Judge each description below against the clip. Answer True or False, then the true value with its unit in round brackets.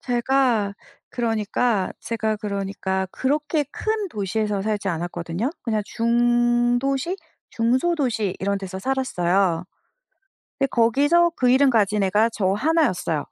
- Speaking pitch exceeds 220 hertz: True (230 Hz)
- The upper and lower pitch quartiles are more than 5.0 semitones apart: False (4.7 semitones)